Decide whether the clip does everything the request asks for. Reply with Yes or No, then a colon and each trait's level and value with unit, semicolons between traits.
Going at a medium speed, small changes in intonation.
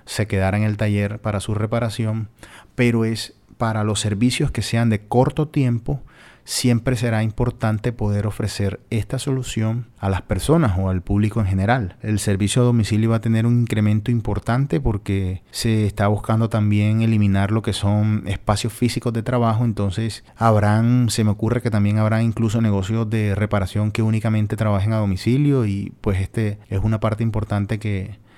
Yes: average, 170 wpm; narrow, 1.9 semitones